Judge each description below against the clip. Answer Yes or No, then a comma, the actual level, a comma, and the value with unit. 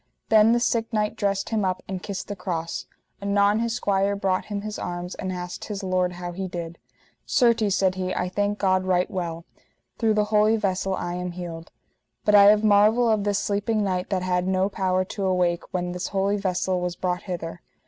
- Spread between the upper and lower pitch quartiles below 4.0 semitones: Yes, narrow, 2.4 semitones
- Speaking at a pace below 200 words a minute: No, fast, 205 wpm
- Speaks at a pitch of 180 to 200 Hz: Yes, high, 190 Hz